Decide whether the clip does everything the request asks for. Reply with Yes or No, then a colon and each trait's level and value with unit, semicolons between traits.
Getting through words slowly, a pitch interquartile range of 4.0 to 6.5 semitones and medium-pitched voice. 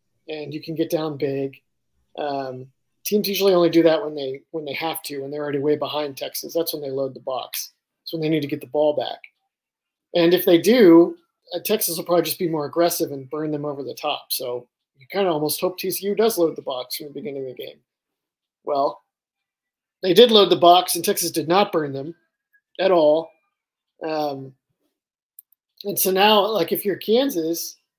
No: fast, 205 wpm; average, 4.3 semitones; medium, 165 Hz